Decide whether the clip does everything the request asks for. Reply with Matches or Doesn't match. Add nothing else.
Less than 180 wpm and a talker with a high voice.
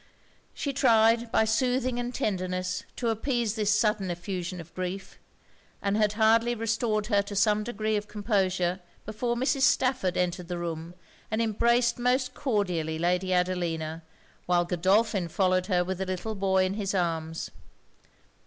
Matches